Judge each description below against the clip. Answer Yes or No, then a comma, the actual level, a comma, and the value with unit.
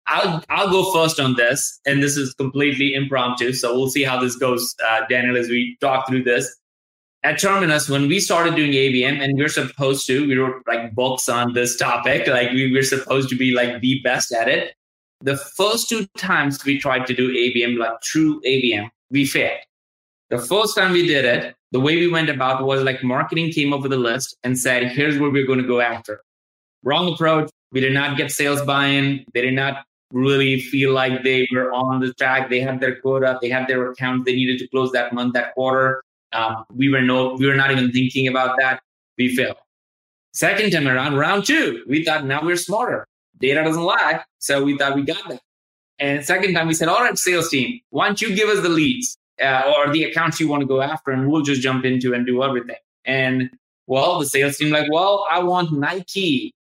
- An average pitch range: Yes, average, 3.0 semitones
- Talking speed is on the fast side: Yes, fast, 215 wpm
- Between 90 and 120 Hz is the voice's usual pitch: No, low, 135 Hz